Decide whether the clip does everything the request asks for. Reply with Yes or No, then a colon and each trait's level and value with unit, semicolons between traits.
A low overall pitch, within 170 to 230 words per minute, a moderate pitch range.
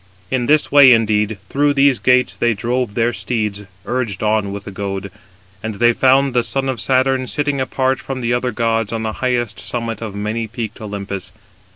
Yes: low, 120 Hz; average, 190 wpm; average, 3.3 semitones